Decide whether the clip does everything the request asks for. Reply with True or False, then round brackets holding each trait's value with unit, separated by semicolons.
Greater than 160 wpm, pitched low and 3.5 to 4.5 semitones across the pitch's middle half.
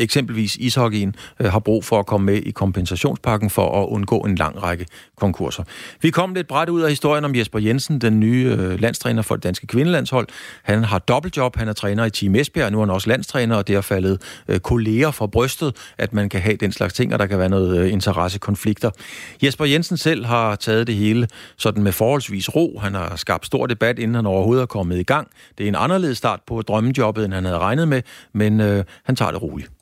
True (215 wpm; 110 Hz; 3.9 semitones)